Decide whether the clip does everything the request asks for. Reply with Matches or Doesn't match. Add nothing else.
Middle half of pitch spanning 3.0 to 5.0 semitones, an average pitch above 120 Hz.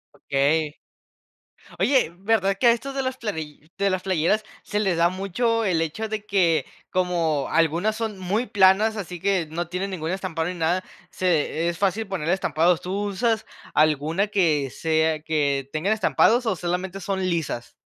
Matches